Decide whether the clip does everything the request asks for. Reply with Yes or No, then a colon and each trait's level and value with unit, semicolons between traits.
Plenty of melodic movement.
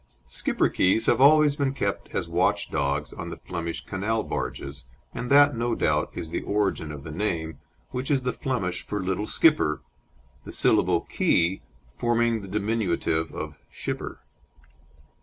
Yes: wide, 6.6 semitones